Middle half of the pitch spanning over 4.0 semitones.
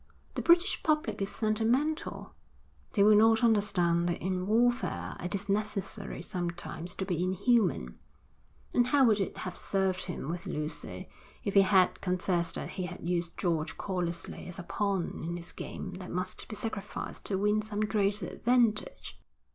No: average, 3.4 semitones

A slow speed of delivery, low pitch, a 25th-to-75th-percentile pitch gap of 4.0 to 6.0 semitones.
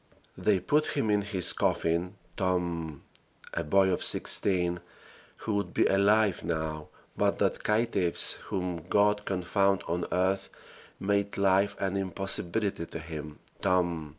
No: slow, 130 wpm; very low, 95 Hz; average, 2.8 semitones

